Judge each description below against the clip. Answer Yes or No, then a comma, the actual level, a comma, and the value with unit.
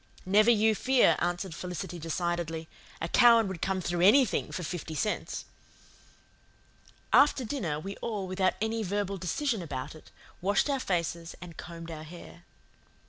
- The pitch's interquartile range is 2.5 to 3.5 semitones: No, average, 4.1 semitones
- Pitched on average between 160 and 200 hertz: Yes, medium, 185 Hz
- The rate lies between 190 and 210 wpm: No, average, 145 wpm